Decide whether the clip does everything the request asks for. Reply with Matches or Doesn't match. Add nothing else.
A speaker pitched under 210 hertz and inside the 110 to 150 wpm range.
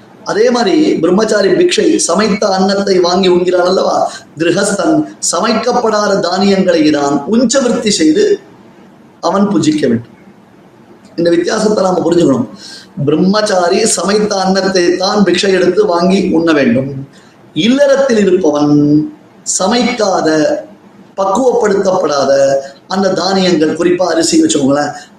Doesn't match